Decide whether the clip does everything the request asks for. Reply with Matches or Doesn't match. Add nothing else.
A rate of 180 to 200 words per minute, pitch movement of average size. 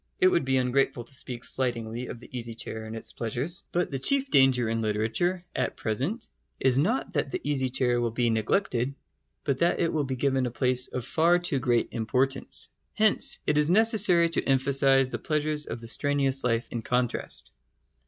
Matches